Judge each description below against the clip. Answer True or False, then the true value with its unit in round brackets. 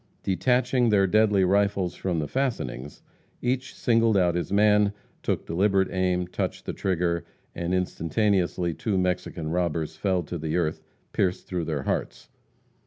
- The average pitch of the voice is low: True (90 Hz)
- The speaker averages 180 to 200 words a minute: False (145 wpm)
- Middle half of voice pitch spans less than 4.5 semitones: True (3.3 semitones)